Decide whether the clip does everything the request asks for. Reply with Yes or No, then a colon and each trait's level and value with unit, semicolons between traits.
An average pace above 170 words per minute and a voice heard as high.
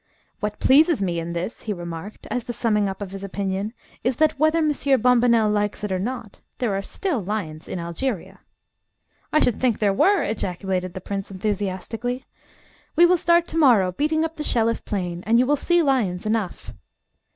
Yes: average, 185 wpm; high, 215 Hz